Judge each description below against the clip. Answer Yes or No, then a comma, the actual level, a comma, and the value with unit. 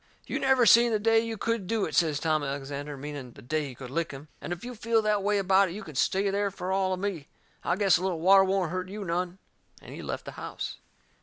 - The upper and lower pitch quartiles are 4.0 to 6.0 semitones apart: Yes, average, 4.9 semitones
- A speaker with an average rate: No, fast, 260 wpm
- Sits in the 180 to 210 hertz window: Yes, medium, 185 Hz